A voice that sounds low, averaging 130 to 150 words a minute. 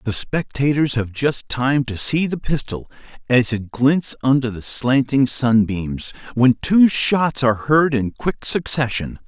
Yes: low, 130 Hz; average, 140 wpm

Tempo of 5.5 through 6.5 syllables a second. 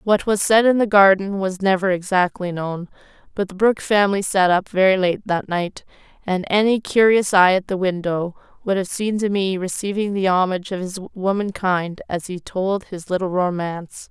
No: 5.0 syllables/s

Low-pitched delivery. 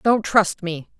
No: high, 195 Hz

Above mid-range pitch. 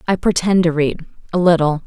No: medium, 170 Hz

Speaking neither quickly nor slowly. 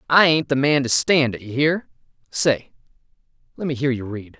Yes: average, 190 wpm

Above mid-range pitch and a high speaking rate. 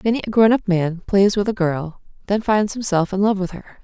Yes: high, 195 Hz; fast, 250 wpm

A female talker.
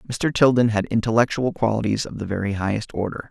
No: male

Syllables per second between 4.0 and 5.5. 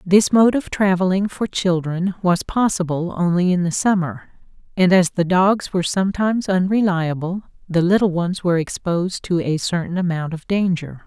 Yes: 5.0 syllables/s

